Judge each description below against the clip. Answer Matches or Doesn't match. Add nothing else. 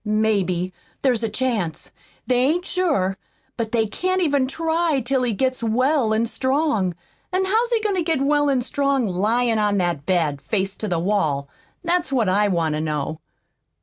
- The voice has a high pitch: Matches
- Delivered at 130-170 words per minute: Doesn't match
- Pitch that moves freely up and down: Matches